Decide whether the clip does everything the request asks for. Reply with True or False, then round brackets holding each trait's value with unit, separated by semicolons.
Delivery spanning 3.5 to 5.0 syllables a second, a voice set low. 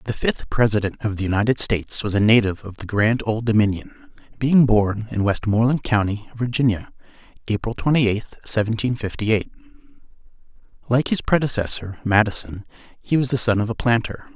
False (5.7 syllables/s; 110 Hz)